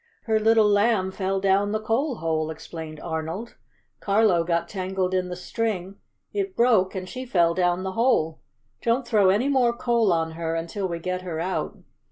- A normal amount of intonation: Yes, average, 4.7 semitones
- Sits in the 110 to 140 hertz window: No, high, 190 Hz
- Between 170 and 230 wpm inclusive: Yes, average, 180 wpm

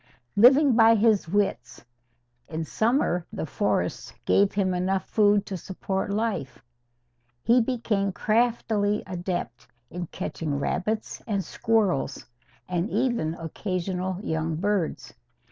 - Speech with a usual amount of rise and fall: Yes, average, 4.0 semitones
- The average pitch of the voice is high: Yes, high, 195 Hz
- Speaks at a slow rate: Yes, slow, 110 wpm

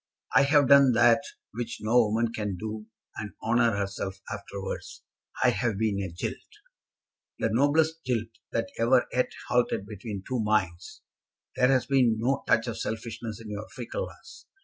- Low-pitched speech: Yes, low, 115 Hz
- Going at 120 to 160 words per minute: Yes, average, 155 wpm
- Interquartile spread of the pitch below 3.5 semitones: Yes, average, 2.8 semitones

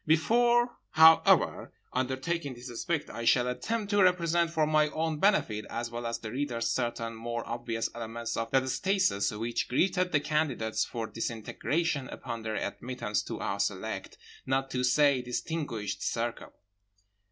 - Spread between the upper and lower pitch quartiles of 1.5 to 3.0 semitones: No, wide, 5.6 semitones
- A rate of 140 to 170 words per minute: Yes, average, 150 wpm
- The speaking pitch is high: No, low, 130 Hz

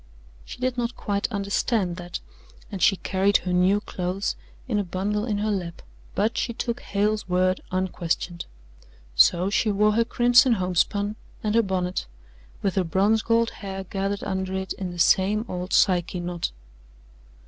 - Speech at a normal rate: Yes, average, 160 wpm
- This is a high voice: Yes, high, 195 Hz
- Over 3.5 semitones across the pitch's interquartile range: No, average, 2.7 semitones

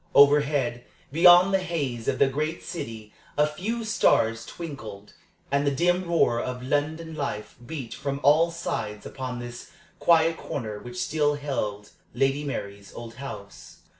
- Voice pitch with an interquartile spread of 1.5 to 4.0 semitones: No, average, 5.3 semitones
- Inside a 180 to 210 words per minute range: No, average, 145 wpm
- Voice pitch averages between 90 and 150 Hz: Yes, medium, 140 Hz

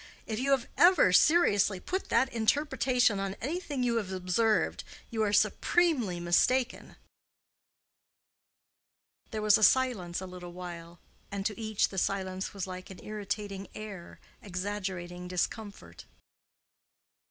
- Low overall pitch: No, high, 205 Hz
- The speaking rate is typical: No, slow, 120 wpm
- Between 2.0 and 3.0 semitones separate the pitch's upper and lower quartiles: No, average, 4.2 semitones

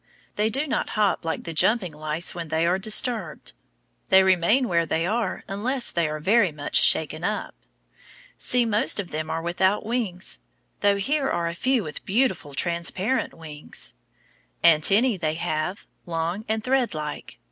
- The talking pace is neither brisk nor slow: Yes, average, 160 wpm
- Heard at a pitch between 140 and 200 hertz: Yes, medium, 185 Hz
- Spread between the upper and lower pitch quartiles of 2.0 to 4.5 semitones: No, average, 5.2 semitones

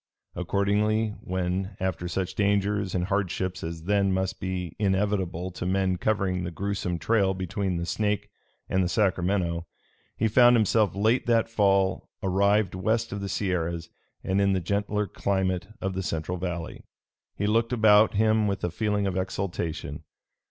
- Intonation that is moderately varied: No, narrow, 2.2 semitones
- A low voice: Yes, very low, 95 Hz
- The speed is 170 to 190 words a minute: No, average, 155 wpm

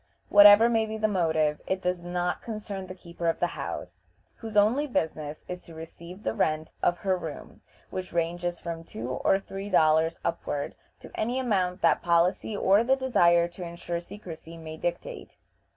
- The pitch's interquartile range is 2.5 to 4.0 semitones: Yes, average, 3.6 semitones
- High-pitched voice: No, medium, 175 Hz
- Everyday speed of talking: Yes, average, 175 wpm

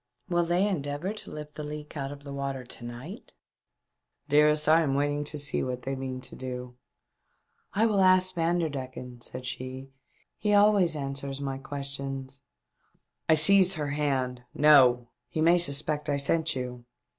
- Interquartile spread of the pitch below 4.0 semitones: Yes, average, 3.4 semitones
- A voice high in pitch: No, medium, 145 Hz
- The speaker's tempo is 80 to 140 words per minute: No, average, 180 wpm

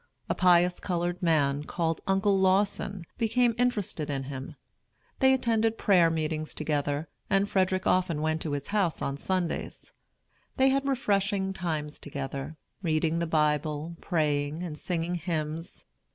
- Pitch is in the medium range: Yes, medium, 170 Hz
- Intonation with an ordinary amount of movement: Yes, average, 4.0 semitones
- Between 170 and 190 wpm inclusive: No, slow, 135 wpm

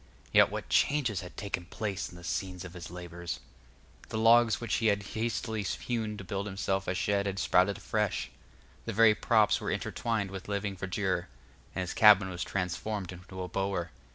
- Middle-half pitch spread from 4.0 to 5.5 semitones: No, average, 2.7 semitones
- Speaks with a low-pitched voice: Yes, low, 100 Hz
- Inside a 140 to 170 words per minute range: No, average, 180 wpm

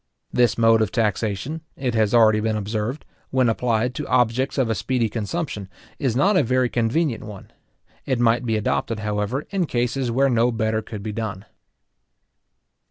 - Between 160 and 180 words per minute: Yes, average, 165 wpm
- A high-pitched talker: No, low, 115 Hz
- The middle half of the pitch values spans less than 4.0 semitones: Yes, average, 2.8 semitones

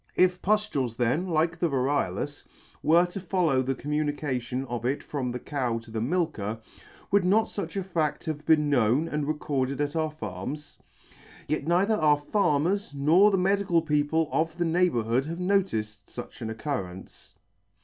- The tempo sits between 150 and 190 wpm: Yes, average, 160 wpm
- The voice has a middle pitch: Yes, medium, 150 Hz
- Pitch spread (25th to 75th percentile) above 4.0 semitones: Yes, average, 5.2 semitones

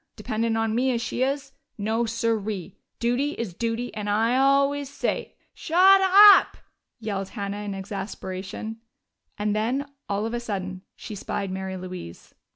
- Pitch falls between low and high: No, high, 225 Hz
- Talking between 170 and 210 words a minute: No, average, 155 wpm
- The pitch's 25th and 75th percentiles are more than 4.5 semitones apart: No, average, 4.2 semitones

